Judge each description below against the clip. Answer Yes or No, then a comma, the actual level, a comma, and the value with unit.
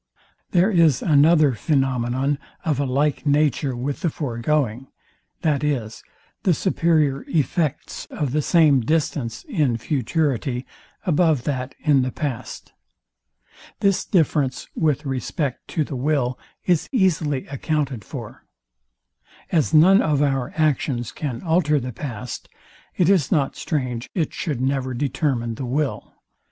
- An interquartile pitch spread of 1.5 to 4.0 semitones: Yes, average, 3.4 semitones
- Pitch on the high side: No, medium, 145 Hz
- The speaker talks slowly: Yes, slow, 125 wpm